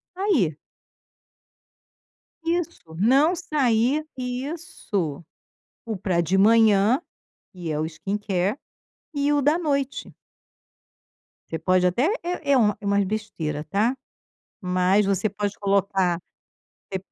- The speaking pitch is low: No, high, 205 Hz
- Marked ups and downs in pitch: Yes, wide, 6.7 semitones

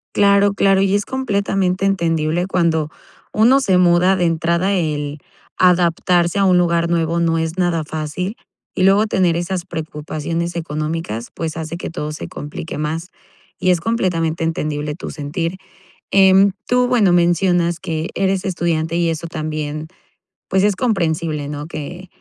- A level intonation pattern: No, average, 3.0 semitones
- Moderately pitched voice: Yes, medium, 170 Hz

